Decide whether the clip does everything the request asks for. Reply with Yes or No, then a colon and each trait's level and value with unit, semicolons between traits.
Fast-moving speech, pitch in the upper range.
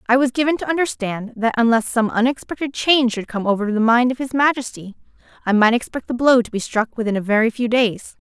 Yes: fast, 225 wpm; high, 240 Hz